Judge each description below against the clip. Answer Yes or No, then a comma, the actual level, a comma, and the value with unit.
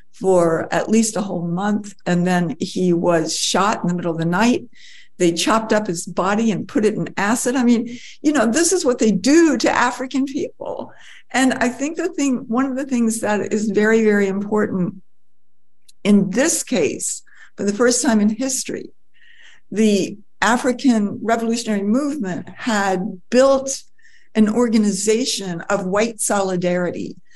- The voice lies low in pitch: No, high, 220 Hz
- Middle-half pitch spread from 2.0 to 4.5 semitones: No, average, 4.9 semitones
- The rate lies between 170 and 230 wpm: No, average, 160 wpm